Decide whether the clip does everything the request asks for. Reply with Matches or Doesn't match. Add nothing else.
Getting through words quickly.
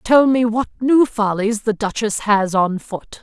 Doesn't match